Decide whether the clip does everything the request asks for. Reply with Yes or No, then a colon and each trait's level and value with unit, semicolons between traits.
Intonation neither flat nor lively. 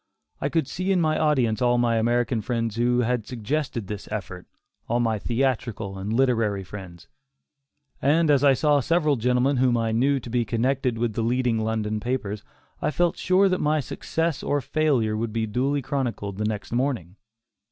Yes: average, 4.1 semitones